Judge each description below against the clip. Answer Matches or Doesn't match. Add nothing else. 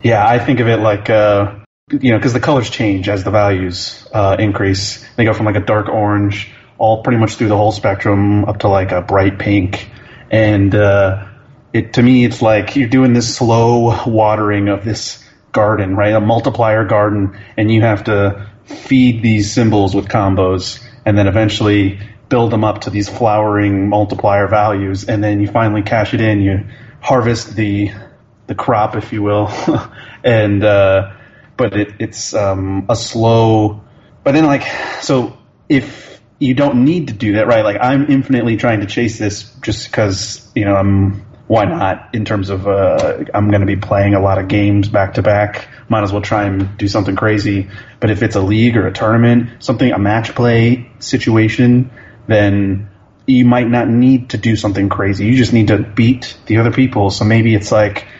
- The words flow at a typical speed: Matches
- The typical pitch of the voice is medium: Doesn't match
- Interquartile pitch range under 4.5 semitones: Matches